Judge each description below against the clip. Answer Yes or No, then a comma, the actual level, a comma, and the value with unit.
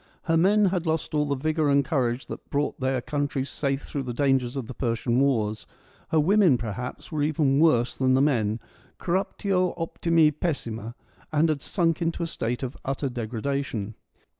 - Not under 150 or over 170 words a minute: No, average, 185 wpm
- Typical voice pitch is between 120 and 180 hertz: Yes, medium, 140 Hz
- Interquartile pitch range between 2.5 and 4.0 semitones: No, average, 4.5 semitones